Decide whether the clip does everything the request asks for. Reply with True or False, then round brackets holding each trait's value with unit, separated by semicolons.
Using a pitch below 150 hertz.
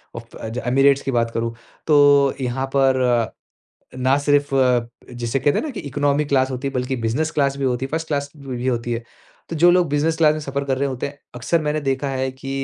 True (135 Hz)